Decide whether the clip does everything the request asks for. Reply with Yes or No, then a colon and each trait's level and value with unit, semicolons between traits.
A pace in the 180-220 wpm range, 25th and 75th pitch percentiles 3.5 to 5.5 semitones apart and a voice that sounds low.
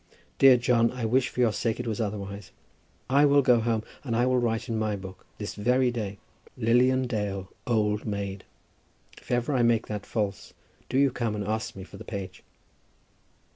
No: average, 190 wpm; average, 3.1 semitones; low, 115 Hz